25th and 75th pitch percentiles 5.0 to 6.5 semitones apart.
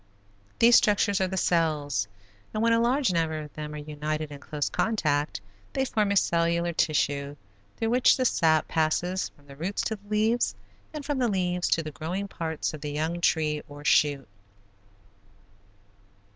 Yes: average, 5.3 semitones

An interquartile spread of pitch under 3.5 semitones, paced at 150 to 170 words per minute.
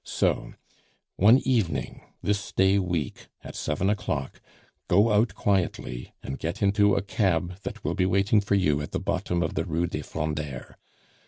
No: average, 4.2 semitones; average, 165 wpm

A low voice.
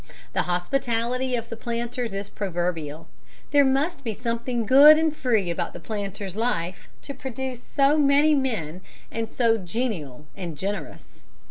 No: high, 230 Hz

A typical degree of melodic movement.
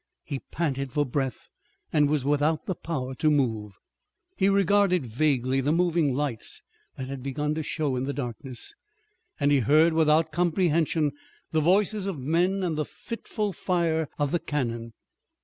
Yes: average, 3.9 semitones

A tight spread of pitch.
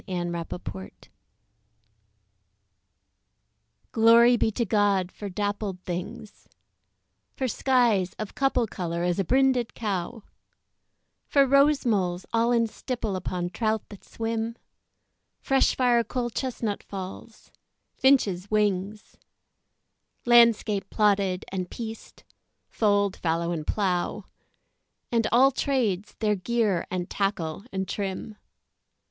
No: average, 4.1 semitones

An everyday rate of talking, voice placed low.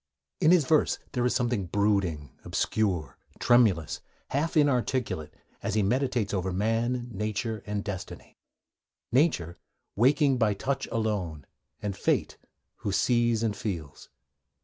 No: slow, 125 wpm; low, 110 Hz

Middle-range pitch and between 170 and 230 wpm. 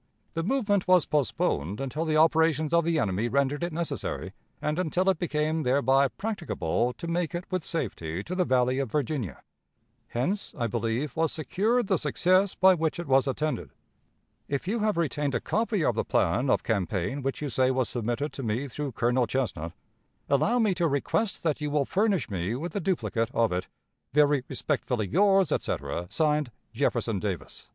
Yes: medium, 145 Hz; average, 180 wpm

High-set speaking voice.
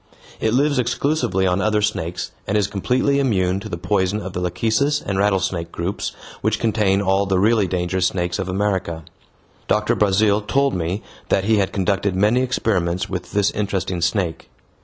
No: low, 100 Hz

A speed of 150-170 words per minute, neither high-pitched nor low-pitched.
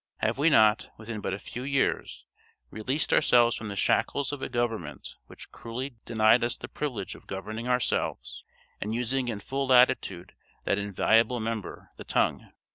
No: average, 165 wpm; low, 115 Hz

